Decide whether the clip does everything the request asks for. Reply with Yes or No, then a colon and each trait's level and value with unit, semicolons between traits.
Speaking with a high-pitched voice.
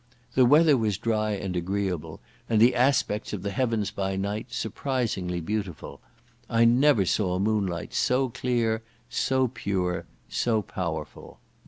No: low, 105 Hz